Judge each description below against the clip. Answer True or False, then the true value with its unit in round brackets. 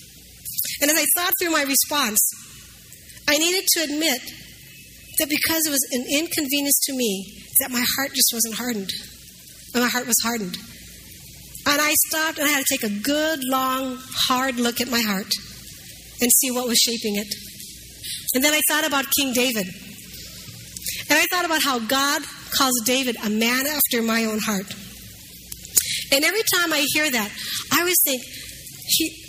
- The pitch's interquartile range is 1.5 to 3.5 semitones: False (4.1 semitones)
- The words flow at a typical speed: True (170 wpm)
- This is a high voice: True (270 Hz)